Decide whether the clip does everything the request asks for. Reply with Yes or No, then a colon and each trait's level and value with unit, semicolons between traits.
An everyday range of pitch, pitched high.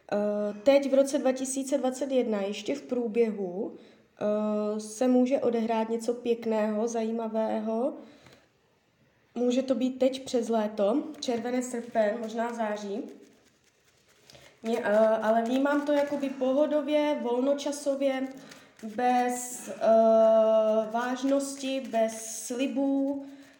Yes: average, 3.4 semitones; high, 245 Hz